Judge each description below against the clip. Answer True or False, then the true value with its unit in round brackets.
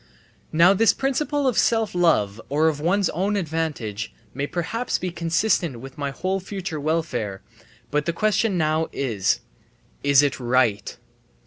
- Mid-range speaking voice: True (160 Hz)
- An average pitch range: False (5.8 semitones)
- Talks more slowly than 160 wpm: True (145 wpm)